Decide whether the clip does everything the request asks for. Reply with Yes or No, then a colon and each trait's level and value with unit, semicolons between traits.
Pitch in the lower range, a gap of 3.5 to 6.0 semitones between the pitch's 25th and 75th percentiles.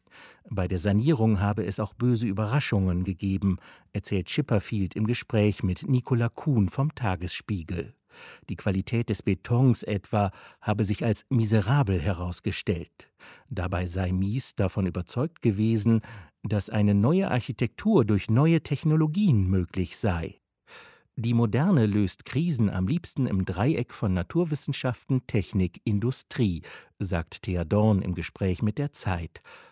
Yes: low, 105 Hz; average, 4.6 semitones